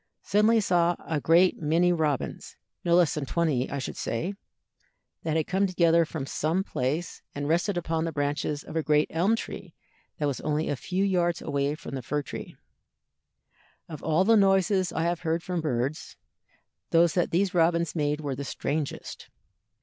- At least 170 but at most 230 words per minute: Yes, average, 180 wpm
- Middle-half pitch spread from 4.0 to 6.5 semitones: No, average, 3.0 semitones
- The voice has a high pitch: No, medium, 165 Hz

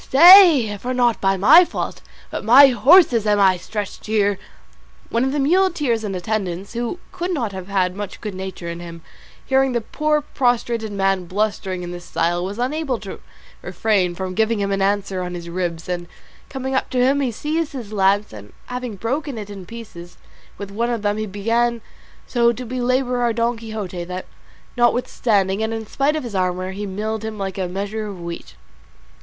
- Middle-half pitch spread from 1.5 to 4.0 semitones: No, average, 4.5 semitones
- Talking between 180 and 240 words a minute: Yes, average, 190 wpm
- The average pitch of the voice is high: Yes, high, 215 Hz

